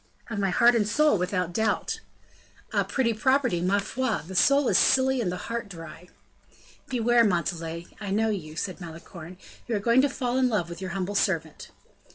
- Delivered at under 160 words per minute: No, average, 190 wpm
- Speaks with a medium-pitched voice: No, high, 205 Hz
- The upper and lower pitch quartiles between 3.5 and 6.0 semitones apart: Yes, average, 5.3 semitones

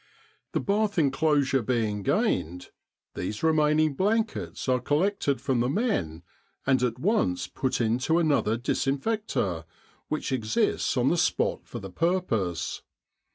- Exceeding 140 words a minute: No, slow, 135 wpm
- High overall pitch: No, low, 135 Hz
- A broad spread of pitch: Yes, wide, 6.4 semitones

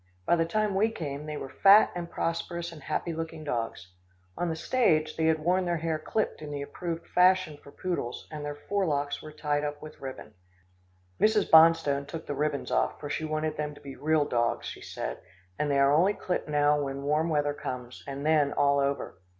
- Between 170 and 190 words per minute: No, fast, 205 wpm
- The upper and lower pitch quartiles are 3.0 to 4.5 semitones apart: No, narrow, 2.6 semitones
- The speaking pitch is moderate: Yes, medium, 155 Hz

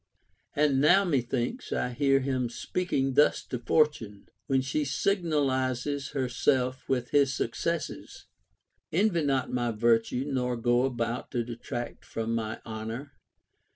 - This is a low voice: Yes, low, 130 Hz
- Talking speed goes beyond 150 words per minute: No, average, 140 wpm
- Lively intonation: No, average, 3.1 semitones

